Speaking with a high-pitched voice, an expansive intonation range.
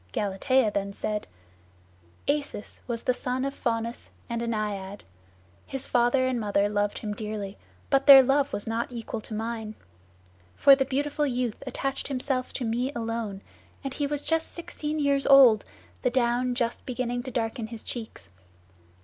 No: high, 240 Hz; average, 3.6 semitones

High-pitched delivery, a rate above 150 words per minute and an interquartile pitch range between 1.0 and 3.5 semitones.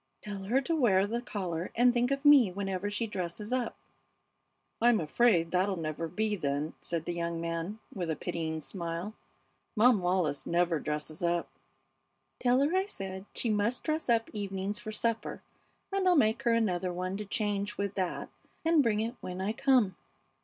No: high, 200 Hz; average, 175 wpm; average, 5.1 semitones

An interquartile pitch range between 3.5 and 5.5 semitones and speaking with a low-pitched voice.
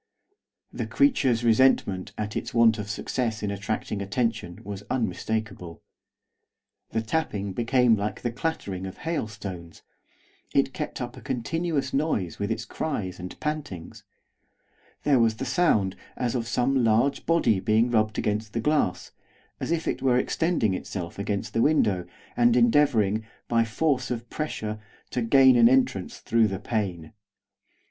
Yes: average, 4.3 semitones; low, 115 Hz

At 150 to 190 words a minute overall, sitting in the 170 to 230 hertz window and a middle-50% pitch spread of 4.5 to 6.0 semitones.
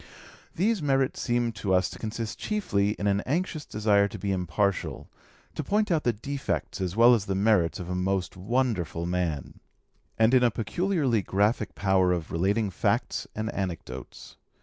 No: average, 170 wpm; low, 105 Hz; average, 4.9 semitones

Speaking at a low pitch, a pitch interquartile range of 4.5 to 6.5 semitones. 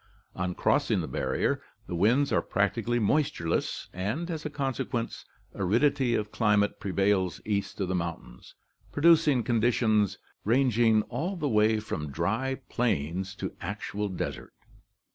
Yes: low, 110 Hz; average, 5.2 semitones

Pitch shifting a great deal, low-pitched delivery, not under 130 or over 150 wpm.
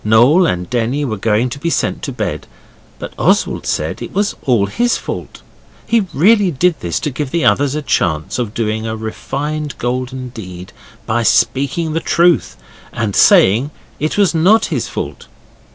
No: wide, 6.3 semitones; low, 130 Hz; average, 170 wpm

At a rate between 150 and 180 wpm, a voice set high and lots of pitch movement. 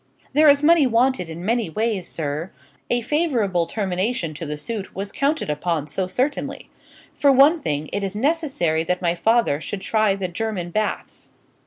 Yes: average, 170 wpm; high, 205 Hz; wide, 6.6 semitones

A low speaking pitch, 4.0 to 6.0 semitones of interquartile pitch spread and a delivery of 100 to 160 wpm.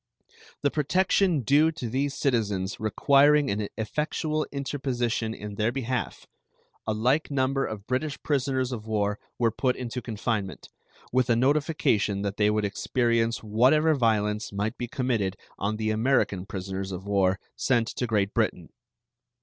Yes: low, 115 Hz; average, 4.5 semitones; average, 145 wpm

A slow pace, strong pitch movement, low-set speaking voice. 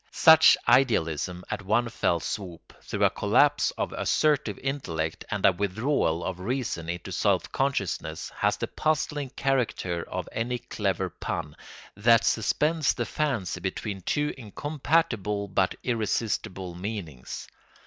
Yes: slow, 130 wpm; wide, 6.7 semitones; low, 105 Hz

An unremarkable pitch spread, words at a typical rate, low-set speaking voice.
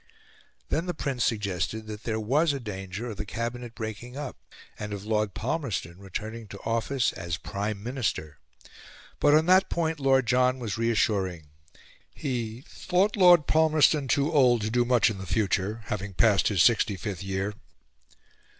Yes: average, 4.8 semitones; average, 160 wpm; low, 115 Hz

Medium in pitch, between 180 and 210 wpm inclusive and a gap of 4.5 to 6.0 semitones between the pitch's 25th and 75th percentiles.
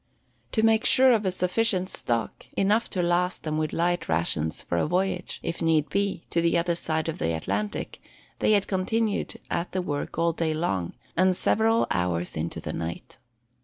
Yes: medium, 170 Hz; average, 185 wpm; average, 4.8 semitones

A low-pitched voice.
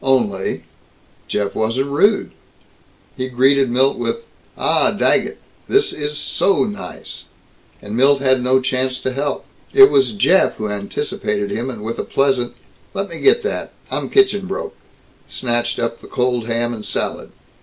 Yes: low, 130 Hz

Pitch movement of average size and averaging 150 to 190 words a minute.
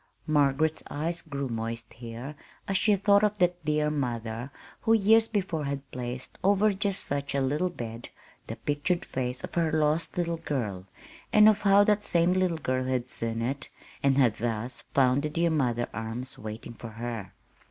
No: wide, 6.5 semitones; average, 175 wpm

